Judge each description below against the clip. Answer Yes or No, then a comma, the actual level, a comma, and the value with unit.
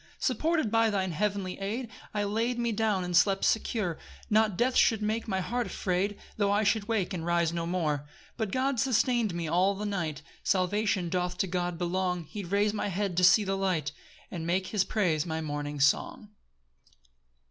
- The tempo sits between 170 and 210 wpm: Yes, average, 190 wpm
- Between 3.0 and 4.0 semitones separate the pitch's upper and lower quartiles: Yes, average, 3.5 semitones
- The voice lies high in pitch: Yes, high, 195 Hz